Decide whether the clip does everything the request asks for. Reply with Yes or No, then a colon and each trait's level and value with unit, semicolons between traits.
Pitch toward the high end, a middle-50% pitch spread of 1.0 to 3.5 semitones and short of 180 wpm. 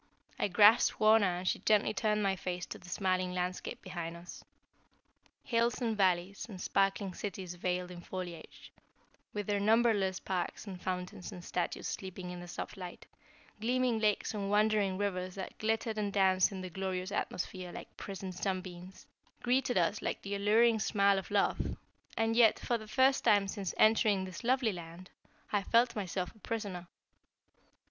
Yes: high, 195 Hz; average, 2.9 semitones; average, 165 wpm